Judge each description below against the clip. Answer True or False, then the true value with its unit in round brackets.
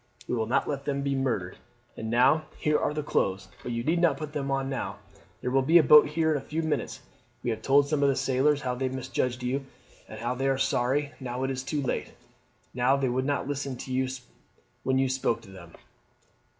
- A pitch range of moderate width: False (2.3 semitones)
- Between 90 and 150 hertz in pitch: True (135 Hz)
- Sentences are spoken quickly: True (220 wpm)